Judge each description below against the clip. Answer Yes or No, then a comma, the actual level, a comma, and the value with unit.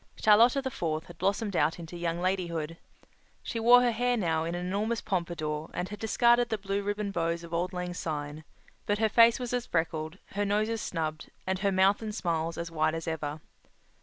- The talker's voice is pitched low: No, medium, 180 Hz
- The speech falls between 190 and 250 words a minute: Yes, fast, 205 wpm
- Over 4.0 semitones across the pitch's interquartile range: Yes, average, 4.4 semitones